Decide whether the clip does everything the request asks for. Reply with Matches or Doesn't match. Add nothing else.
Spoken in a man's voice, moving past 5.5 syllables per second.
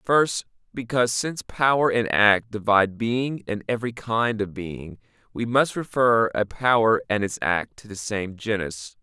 Doesn't match